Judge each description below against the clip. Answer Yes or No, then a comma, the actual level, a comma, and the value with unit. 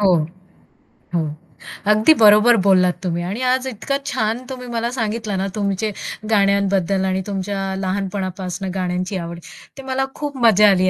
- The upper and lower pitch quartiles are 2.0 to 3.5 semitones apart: Yes, average, 2.9 semitones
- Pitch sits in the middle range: No, high, 200 Hz